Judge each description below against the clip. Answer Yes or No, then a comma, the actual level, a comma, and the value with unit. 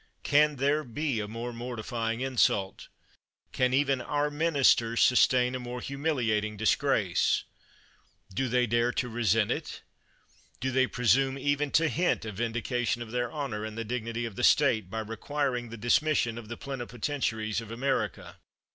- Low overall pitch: Yes, low, 120 Hz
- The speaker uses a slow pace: No, average, 155 wpm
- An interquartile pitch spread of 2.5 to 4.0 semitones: Yes, average, 3.2 semitones